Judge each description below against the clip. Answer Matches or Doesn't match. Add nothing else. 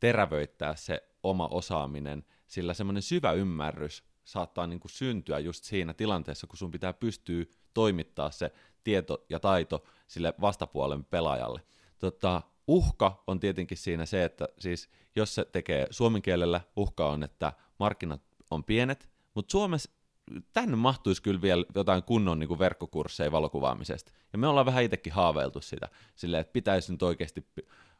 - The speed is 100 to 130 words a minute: Doesn't match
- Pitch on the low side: Matches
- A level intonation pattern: Doesn't match